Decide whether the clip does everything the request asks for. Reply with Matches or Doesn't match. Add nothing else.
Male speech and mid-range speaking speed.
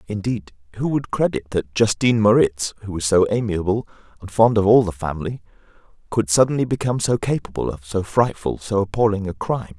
Matches